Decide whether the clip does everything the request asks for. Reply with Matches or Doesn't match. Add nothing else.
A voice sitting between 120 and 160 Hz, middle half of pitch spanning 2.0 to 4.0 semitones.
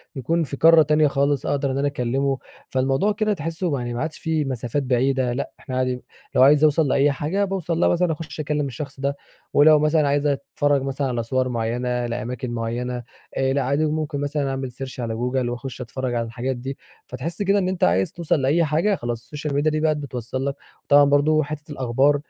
Matches